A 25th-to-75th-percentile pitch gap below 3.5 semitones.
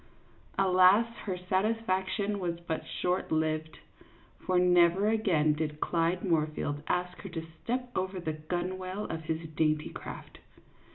Yes: average, 2.9 semitones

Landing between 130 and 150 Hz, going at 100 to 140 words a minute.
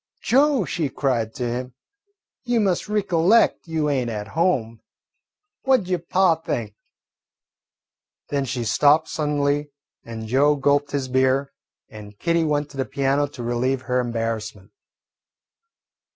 Yes: medium, 140 Hz; slow, 135 wpm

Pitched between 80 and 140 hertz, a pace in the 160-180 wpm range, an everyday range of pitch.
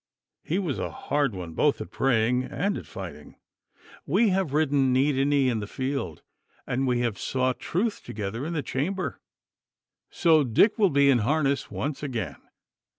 Yes: low, 135 Hz; average, 170 wpm; average, 3.8 semitones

